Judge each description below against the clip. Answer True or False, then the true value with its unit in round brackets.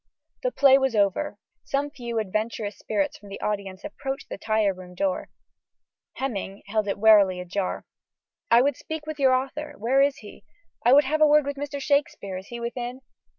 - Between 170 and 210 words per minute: True (185 wpm)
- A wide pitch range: True (5.7 semitones)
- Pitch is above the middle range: True (240 Hz)